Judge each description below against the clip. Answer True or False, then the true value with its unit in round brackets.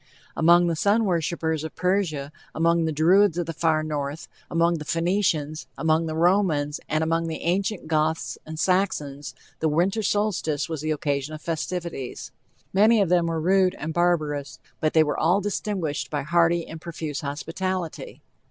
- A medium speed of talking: True (165 wpm)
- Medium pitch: True (165 Hz)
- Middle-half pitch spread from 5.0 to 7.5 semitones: False (2.5 semitones)